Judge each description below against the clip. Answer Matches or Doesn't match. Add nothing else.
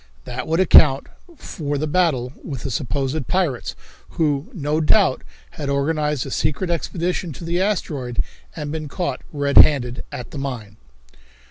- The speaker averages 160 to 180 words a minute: Doesn't match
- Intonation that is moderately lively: Matches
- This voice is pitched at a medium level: Matches